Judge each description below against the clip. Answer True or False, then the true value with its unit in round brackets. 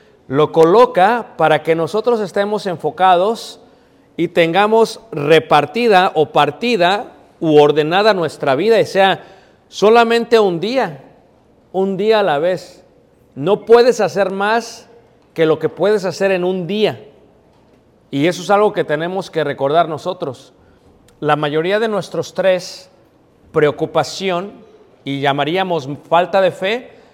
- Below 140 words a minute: True (130 wpm)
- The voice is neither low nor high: True (180 Hz)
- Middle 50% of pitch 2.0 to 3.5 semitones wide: False (5.0 semitones)